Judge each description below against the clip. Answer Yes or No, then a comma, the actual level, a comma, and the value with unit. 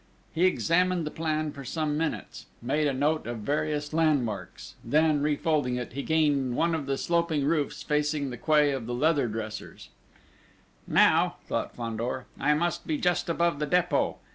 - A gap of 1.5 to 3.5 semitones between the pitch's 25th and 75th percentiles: Yes, average, 2.9 semitones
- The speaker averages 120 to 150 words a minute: No, average, 165 wpm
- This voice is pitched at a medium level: Yes, medium, 150 Hz